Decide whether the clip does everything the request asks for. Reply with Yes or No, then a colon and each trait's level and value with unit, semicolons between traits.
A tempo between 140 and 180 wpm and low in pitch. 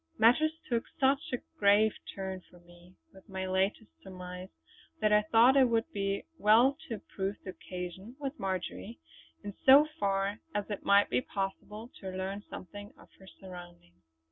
No: average, 165 wpm; high, 200 Hz